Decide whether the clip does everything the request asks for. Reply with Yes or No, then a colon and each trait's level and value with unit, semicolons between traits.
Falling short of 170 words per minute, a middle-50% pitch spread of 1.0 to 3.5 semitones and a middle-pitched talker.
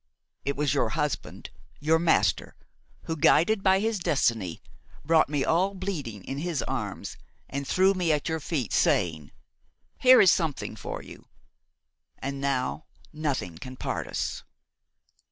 No: slow, 135 wpm; average, 4.6 semitones; medium, 150 Hz